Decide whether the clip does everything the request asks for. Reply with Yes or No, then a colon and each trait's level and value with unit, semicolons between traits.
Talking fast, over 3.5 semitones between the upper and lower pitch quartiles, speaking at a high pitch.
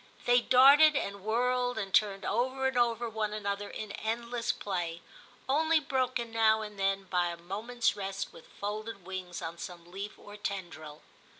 No: average, 165 wpm; average, 3.9 semitones; high, 215 Hz